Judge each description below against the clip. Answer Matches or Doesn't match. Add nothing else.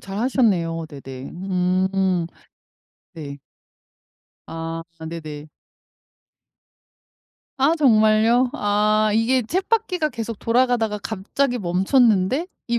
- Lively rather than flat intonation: Matches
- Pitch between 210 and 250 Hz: Matches